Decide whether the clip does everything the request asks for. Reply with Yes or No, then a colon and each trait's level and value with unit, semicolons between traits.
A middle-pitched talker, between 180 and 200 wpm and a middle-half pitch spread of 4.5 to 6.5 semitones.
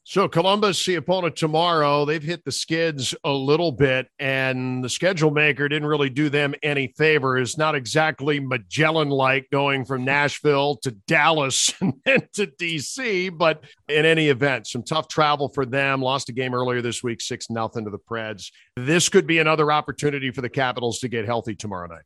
No: medium, 145 Hz; average, 190 wpm; average, 3.4 semitones